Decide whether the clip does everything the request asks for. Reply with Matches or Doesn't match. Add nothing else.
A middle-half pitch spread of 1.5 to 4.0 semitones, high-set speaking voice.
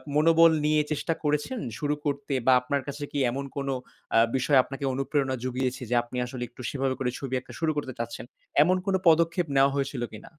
Doesn't match